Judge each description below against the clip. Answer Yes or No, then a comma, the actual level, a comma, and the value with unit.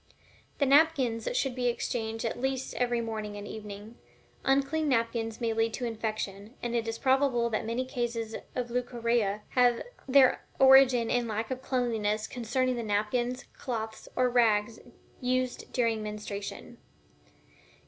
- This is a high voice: Yes, high, 235 Hz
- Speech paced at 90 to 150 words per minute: Yes, average, 140 wpm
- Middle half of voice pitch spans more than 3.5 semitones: No, narrow, 2.4 semitones